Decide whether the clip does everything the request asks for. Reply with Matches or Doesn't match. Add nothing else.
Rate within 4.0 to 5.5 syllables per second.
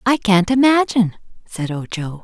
Matches